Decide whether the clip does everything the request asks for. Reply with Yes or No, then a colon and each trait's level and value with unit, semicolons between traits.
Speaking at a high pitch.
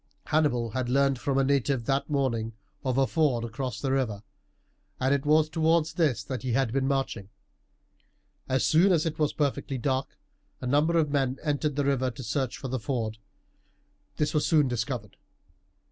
No: low, 135 Hz